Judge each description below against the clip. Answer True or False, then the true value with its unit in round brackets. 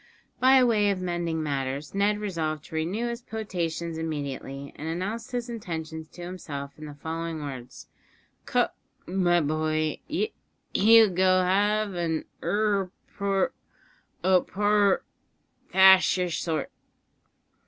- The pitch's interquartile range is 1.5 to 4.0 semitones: False (4.6 semitones)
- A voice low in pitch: False (180 Hz)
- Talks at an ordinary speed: False (125 wpm)